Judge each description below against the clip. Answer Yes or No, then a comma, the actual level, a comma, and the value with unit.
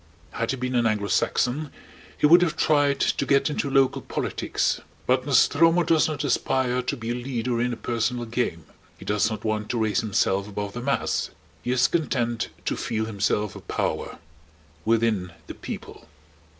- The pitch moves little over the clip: No, average, 3.8 semitones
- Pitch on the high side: No, low, 120 Hz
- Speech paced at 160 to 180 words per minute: Yes, average, 175 wpm